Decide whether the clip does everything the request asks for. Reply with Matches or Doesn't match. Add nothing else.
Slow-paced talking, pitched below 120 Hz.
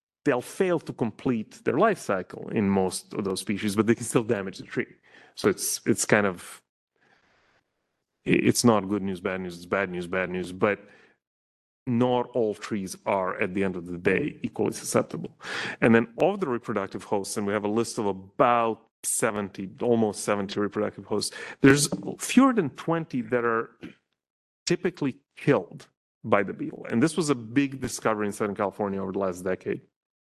Doesn't match